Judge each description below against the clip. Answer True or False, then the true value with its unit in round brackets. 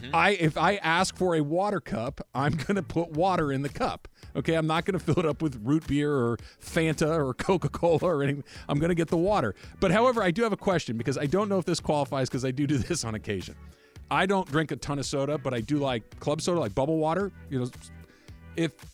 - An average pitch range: True (4.3 semitones)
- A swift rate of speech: True (250 wpm)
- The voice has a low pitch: False (150 Hz)